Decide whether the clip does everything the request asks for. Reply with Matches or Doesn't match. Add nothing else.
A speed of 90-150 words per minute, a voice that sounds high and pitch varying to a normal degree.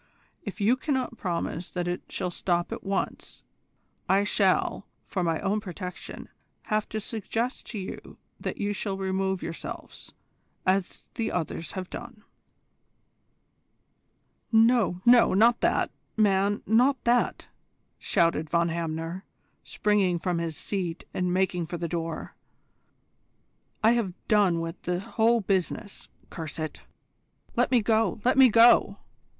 Matches